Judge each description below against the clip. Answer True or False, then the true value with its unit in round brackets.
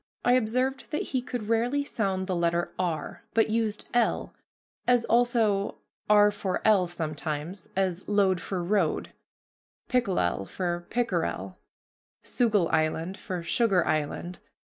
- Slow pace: True (125 wpm)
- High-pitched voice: True (195 Hz)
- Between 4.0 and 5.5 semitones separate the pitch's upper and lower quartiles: True (4.9 semitones)